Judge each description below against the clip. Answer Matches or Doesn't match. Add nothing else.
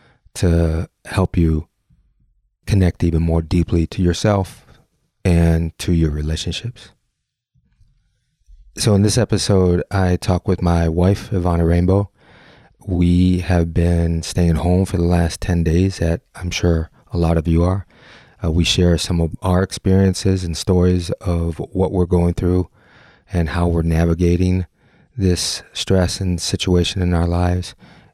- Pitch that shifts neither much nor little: Doesn't match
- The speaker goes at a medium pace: Matches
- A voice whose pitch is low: Matches